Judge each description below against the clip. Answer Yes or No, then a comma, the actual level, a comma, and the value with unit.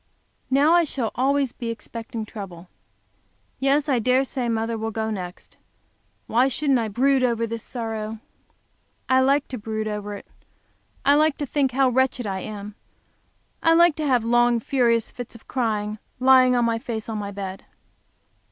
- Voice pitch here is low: No, high, 235 Hz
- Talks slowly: No, average, 170 wpm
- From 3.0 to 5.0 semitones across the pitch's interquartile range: Yes, average, 3.3 semitones